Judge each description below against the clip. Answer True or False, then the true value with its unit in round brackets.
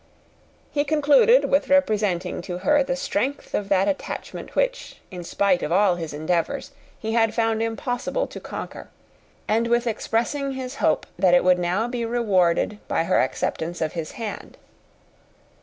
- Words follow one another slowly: False (155 wpm)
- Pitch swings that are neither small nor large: False (6.5 semitones)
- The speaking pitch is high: True (220 Hz)